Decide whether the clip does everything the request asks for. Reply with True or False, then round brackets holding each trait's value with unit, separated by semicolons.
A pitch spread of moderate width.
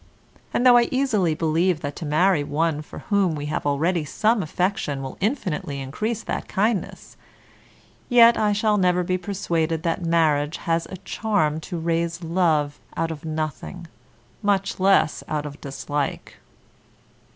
True (4.4 semitones)